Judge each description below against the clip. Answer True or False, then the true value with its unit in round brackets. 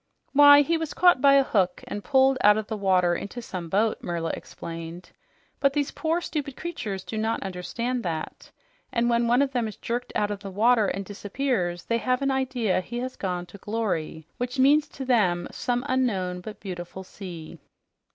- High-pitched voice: True (225 Hz)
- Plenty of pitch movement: True (5.9 semitones)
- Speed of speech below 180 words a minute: False (190 wpm)